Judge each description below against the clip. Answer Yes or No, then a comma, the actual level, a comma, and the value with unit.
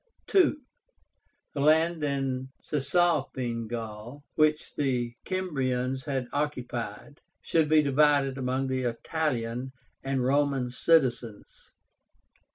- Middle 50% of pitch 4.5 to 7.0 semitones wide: No, average, 3.2 semitones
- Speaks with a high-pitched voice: No, low, 135 Hz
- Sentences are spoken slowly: Yes, slow, 95 wpm